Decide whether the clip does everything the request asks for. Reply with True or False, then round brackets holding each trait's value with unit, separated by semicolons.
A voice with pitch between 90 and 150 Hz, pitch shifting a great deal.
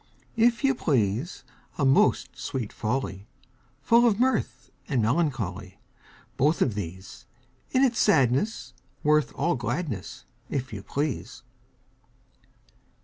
True (135 Hz; 8.8 semitones)